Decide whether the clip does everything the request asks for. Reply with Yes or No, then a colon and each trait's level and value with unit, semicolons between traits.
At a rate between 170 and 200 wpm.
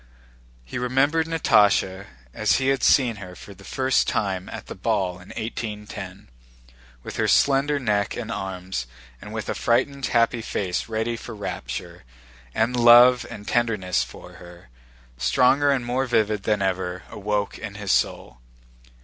No: average, 150 wpm